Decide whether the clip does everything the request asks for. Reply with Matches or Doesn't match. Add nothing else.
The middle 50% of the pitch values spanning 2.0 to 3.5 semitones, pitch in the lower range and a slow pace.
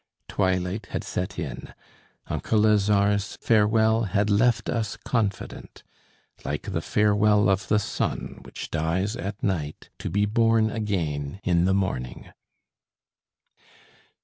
Matches